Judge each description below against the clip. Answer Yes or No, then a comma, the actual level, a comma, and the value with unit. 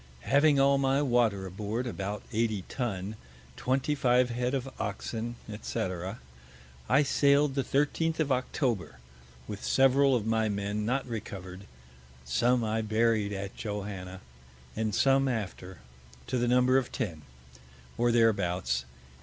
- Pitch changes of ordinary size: Yes, average, 4.5 semitones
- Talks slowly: Yes, slow, 130 wpm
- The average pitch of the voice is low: Yes, low, 115 Hz